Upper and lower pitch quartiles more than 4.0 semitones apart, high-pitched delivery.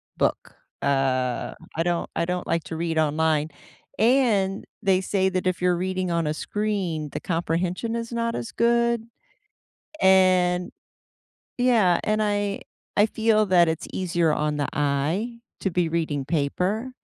No: average, 4.4 semitones; medium, 180 Hz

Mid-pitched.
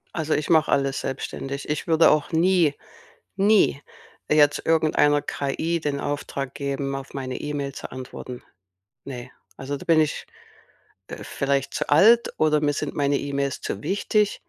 Yes: medium, 145 Hz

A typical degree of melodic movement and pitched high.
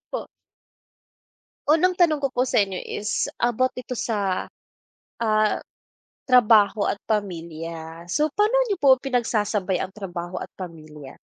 No: wide, 6.1 semitones; high, 215 Hz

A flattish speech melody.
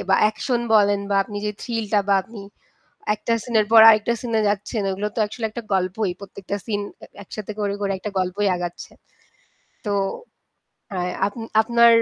Yes: narrow, 1.9 semitones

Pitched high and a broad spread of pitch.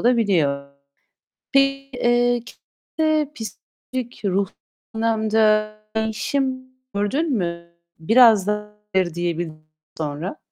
Yes: high, 220 Hz; wide, 5.8 semitones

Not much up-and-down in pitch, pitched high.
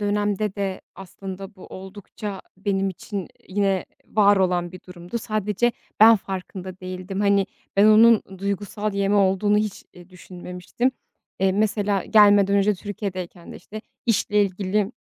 Yes: narrow, 1.8 semitones; high, 200 Hz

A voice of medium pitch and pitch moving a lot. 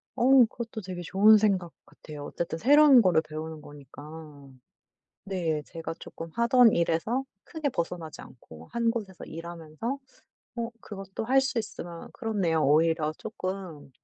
Yes: medium, 180 Hz; wide, 6.1 semitones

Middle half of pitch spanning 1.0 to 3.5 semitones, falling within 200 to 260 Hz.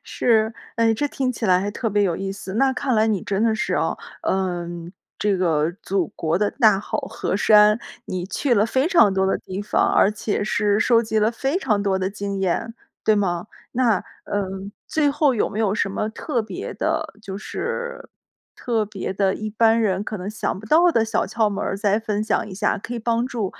Yes: average, 2.8 semitones; high, 210 Hz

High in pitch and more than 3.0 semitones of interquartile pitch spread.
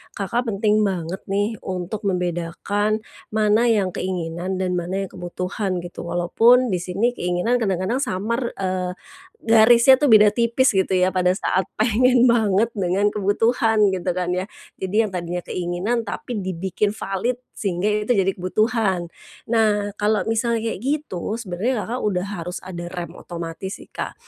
Yes: high, 200 Hz; average, 3.6 semitones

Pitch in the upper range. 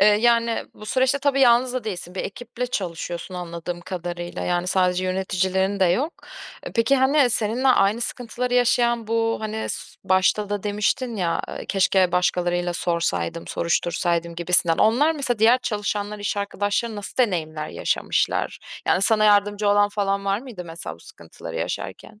Yes: high, 205 Hz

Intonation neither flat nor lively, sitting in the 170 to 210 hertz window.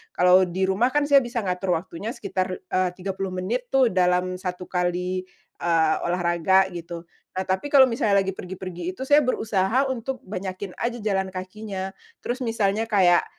Yes: average, 3.7 semitones; high, 190 Hz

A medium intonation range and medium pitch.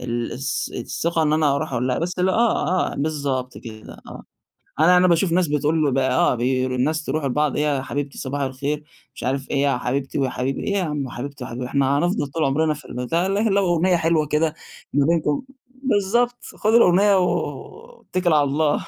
Yes: average, 4.4 semitones; medium, 150 Hz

